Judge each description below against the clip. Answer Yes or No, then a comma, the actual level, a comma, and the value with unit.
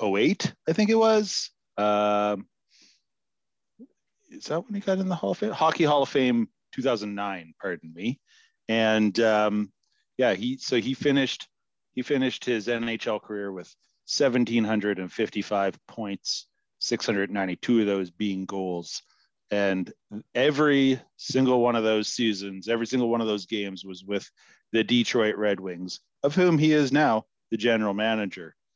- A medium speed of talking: Yes, average, 145 wpm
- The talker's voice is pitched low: Yes, low, 110 Hz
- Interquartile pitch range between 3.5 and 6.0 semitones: Yes, average, 4.8 semitones